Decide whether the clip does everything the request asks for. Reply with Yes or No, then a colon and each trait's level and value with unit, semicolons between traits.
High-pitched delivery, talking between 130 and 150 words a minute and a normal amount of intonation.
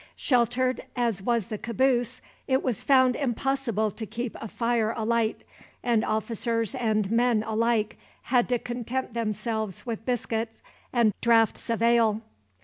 No: high, 230 Hz; average, 140 wpm; narrow, 2.0 semitones